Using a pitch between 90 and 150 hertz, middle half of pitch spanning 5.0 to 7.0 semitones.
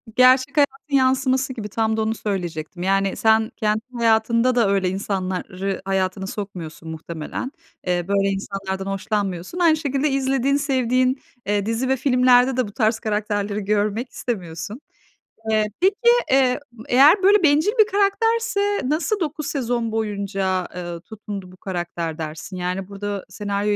No: high, 215 Hz; average, 5.3 semitones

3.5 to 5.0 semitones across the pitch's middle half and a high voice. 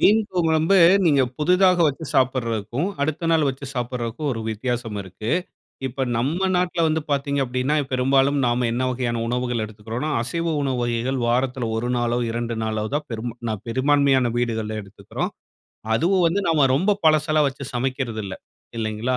No: average, 4.2 semitones; low, 130 Hz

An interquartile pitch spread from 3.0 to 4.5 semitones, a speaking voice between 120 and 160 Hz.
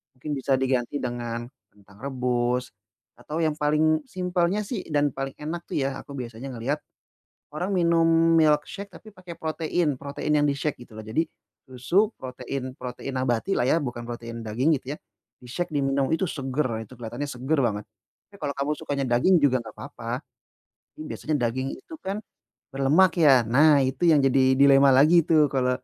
Yes: average, 3.9 semitones; medium, 140 Hz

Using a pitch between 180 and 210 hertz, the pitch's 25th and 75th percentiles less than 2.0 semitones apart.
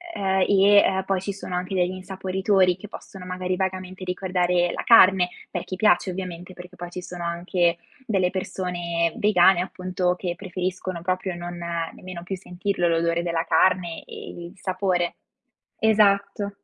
Yes: medium, 185 Hz; narrow, 1.5 semitones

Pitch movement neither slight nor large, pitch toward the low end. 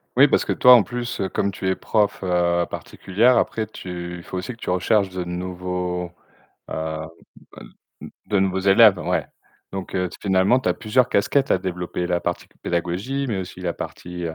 Yes: average, 3.1 semitones; very low, 95 Hz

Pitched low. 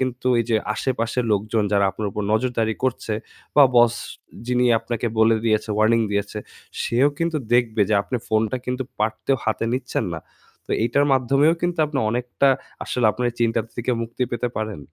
Yes: low, 120 Hz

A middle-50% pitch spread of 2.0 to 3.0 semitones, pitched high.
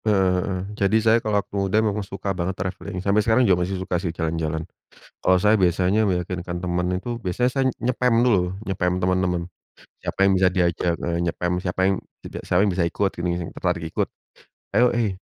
No: narrow, 2.6 semitones; very low, 95 Hz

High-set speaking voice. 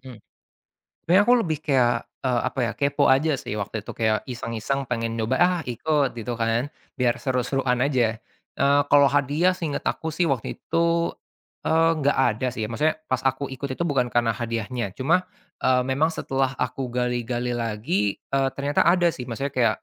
No: low, 130 Hz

